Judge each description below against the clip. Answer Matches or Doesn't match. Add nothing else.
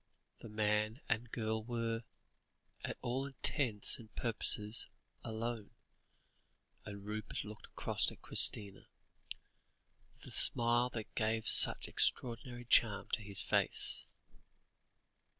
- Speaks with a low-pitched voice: Matches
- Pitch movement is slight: Matches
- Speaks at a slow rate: Matches